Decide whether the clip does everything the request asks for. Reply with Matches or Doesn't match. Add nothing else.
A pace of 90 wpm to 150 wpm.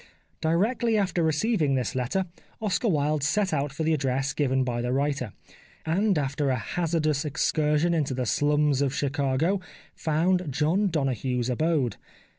Matches